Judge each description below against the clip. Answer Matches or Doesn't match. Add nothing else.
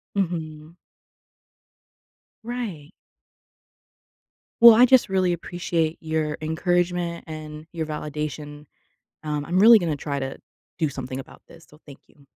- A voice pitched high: Doesn't match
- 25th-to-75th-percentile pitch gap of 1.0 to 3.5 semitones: Matches